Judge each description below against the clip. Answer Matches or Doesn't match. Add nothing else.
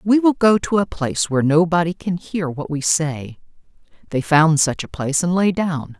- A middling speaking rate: Doesn't match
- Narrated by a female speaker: Matches